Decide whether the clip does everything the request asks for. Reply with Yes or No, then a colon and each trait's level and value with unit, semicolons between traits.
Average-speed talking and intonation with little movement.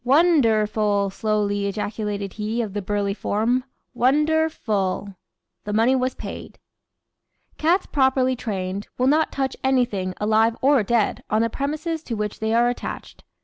No: average, 150 wpm; average, 4.2 semitones